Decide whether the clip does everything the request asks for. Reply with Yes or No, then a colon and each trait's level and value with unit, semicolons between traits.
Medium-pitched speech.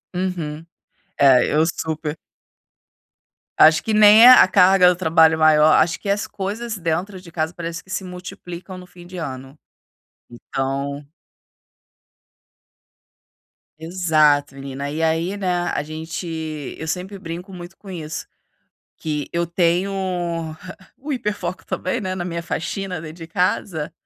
Yes: medium, 170 Hz